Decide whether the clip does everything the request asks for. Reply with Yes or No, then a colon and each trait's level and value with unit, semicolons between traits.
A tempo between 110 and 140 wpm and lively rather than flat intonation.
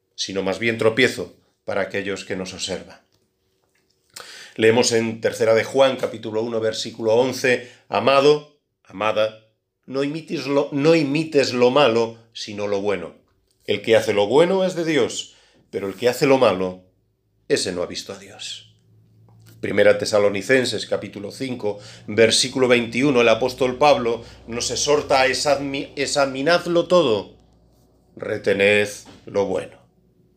No: average, 135 wpm; average, 4.6 semitones